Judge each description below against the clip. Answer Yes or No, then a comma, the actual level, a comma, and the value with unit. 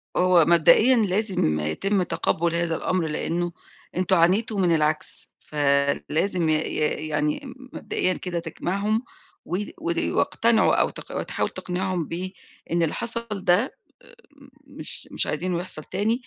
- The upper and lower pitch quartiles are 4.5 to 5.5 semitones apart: No, average, 3.7 semitones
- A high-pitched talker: No, medium, 175 Hz